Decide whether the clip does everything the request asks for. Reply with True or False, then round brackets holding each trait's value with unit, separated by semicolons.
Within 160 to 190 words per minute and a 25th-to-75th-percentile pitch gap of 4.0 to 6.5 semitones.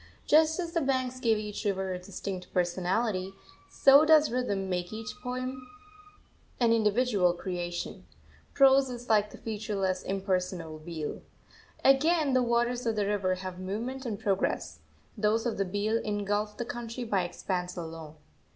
False (150 wpm; 4.9 semitones)